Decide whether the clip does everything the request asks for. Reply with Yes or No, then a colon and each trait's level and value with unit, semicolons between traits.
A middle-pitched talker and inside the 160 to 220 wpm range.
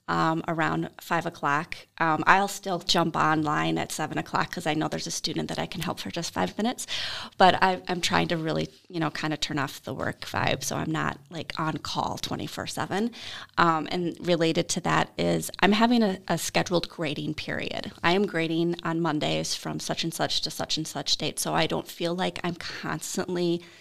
Yes: medium, 170 Hz; fast, 205 wpm